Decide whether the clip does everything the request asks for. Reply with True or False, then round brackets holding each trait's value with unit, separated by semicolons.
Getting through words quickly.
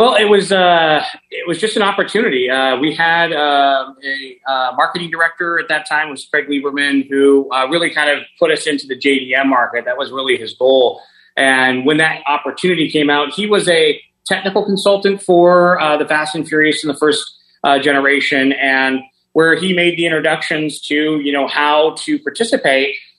False (190 wpm)